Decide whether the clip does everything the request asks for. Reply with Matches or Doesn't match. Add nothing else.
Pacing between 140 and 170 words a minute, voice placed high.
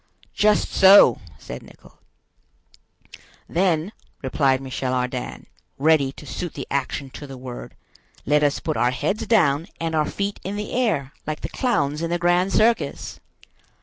Doesn't match